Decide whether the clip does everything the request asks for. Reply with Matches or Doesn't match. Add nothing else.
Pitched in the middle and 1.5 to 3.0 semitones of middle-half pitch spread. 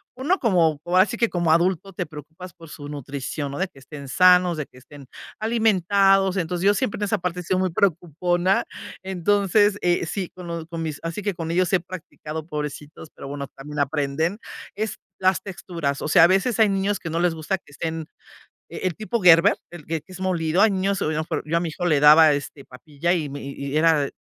Doesn't match